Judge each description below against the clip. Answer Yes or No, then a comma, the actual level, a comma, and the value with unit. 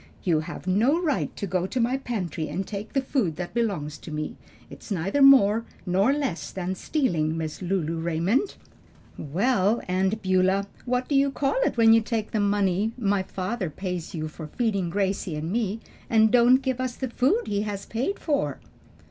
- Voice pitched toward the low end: No, high, 200 Hz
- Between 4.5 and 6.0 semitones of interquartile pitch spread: Yes, average, 5.3 semitones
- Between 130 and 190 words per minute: Yes, average, 185 wpm